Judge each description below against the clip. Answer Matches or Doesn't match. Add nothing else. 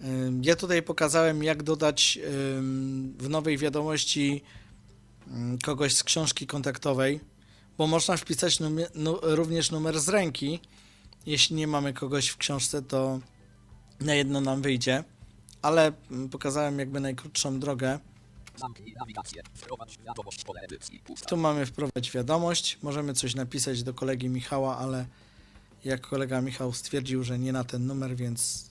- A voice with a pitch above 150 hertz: Doesn't match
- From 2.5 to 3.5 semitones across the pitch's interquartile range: Matches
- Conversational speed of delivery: Matches